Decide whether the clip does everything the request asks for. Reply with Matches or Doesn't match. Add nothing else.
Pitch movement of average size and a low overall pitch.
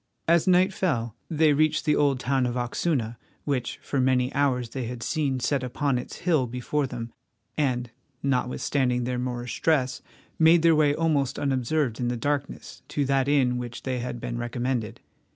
Matches